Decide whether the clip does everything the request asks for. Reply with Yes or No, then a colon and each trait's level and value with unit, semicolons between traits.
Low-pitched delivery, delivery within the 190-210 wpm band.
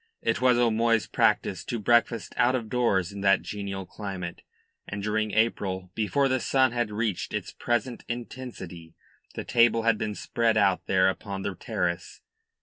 No: low, 110 Hz; average, 160 wpm